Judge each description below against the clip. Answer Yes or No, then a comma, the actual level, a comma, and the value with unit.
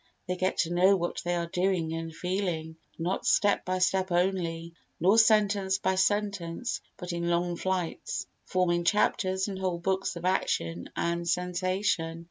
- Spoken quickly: No, average, 155 wpm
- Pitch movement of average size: No, narrow, 1.9 semitones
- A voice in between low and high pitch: Yes, medium, 180 Hz